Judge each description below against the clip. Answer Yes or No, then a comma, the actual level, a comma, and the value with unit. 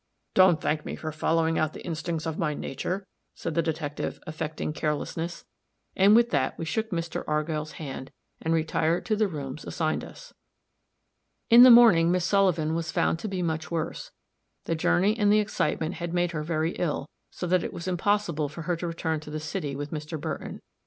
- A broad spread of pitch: No, narrow, 2.6 semitones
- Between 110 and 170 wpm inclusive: No, average, 195 wpm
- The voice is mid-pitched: Yes, medium, 165 Hz